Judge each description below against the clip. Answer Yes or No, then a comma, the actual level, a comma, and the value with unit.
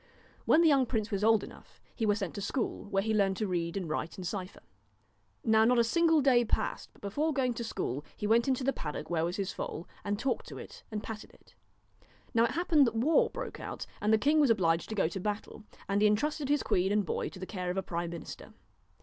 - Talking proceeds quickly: Yes, fast, 245 wpm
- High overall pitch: Yes, high, 215 Hz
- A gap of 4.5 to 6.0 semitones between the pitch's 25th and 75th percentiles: Yes, average, 4.8 semitones